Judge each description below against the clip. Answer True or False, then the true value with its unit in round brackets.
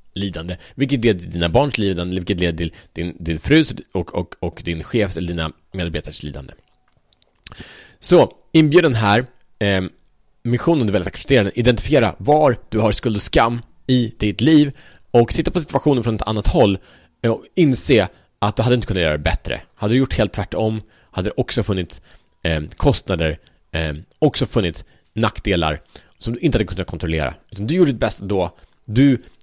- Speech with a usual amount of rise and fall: False (6.2 semitones)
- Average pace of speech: True (180 wpm)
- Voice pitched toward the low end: True (105 Hz)